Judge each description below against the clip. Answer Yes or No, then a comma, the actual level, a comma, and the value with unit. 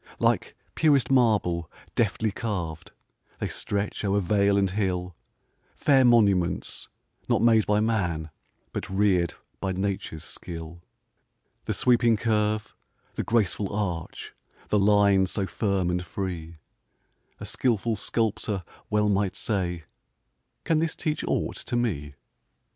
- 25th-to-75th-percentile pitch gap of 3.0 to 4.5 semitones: Yes, average, 3.5 semitones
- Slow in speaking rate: Yes, slow, 120 wpm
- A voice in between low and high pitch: No, low, 100 Hz